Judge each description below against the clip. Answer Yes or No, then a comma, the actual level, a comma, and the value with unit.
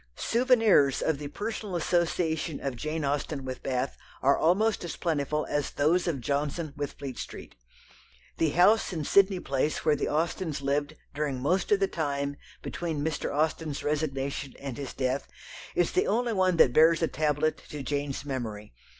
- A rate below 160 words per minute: No, average, 165 wpm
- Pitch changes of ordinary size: Yes, average, 3.5 semitones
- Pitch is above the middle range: No, medium, 150 Hz